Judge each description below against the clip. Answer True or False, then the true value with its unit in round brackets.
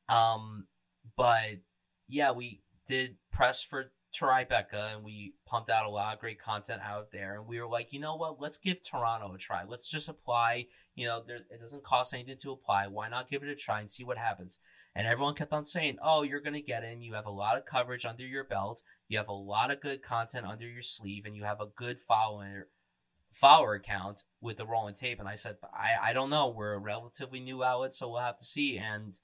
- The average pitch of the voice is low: True (115 Hz)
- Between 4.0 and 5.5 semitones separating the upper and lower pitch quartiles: True (4.5 semitones)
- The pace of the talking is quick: True (230 wpm)